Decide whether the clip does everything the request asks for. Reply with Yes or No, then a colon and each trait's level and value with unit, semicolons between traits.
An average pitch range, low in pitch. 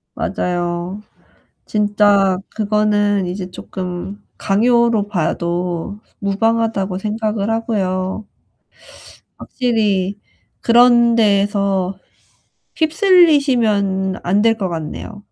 No: average, 3.1 semitones; high, 205 Hz